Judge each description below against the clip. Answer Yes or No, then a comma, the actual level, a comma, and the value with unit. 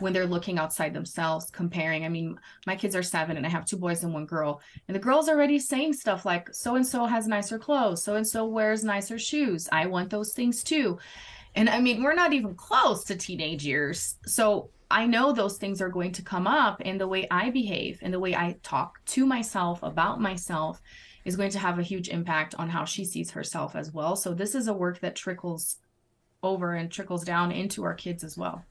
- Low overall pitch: No, medium, 185 Hz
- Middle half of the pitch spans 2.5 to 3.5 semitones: No, average, 4.3 semitones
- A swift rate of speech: Yes, fast, 220 wpm